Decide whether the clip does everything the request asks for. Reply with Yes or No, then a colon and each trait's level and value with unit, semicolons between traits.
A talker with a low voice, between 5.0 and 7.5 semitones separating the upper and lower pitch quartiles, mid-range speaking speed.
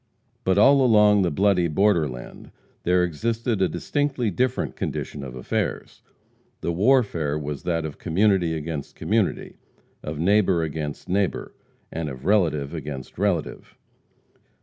No: very low, 90 Hz; average, 5.3 semitones; slow, 125 wpm